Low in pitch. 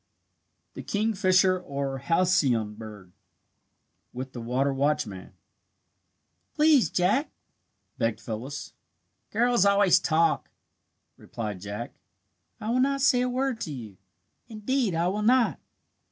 No: medium, 175 Hz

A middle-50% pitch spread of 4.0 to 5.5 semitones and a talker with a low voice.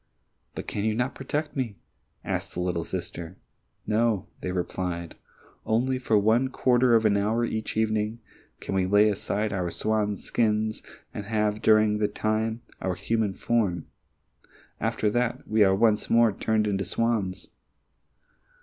No: narrow, 2.6 semitones; low, 110 Hz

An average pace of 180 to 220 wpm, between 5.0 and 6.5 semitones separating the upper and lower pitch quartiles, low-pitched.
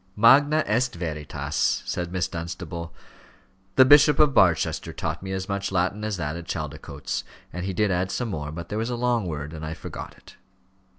Yes: average, 190 wpm; wide, 5.4 semitones; very low, 95 Hz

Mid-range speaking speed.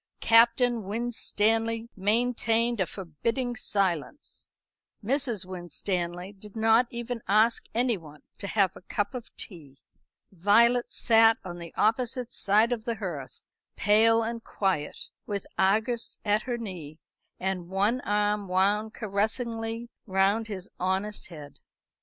No: slow, 125 wpm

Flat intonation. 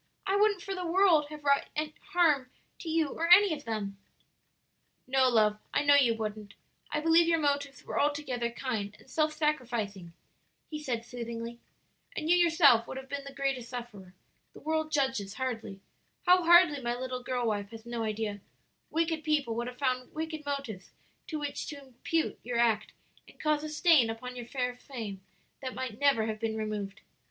No: average, 5.0 semitones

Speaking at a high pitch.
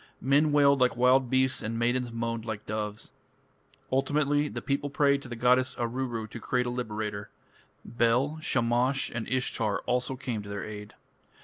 No: low, 125 Hz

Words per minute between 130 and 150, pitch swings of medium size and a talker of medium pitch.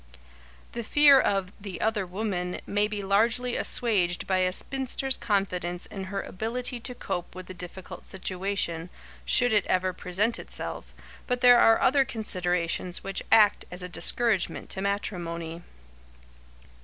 No: average, 145 wpm; average, 3.9 semitones; high, 195 Hz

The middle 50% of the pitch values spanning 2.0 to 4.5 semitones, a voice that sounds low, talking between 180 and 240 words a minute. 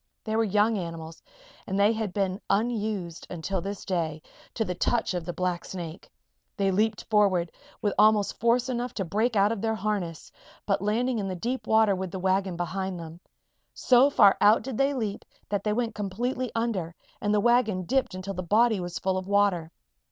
No: average, 3.4 semitones; high, 200 Hz; average, 190 wpm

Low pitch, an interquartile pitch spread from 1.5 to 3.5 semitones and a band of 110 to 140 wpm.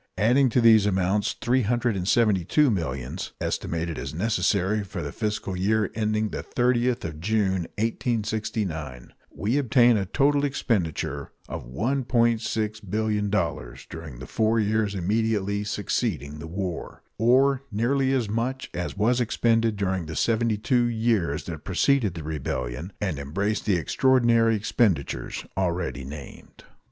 No: low, 105 Hz; average, 4.9 semitones; slow, 135 wpm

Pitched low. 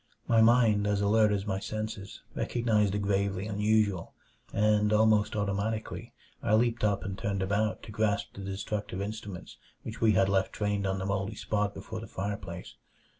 Yes: low, 105 Hz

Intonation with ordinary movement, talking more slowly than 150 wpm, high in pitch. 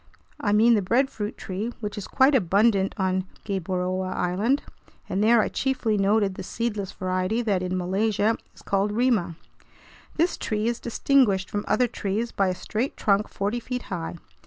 No: average, 3.6 semitones; average, 165 wpm; high, 205 Hz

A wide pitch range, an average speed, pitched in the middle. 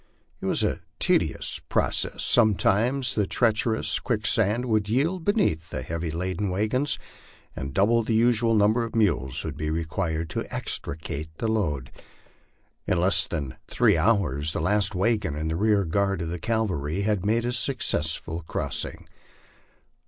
No: wide, 5.8 semitones; average, 155 wpm; low, 100 Hz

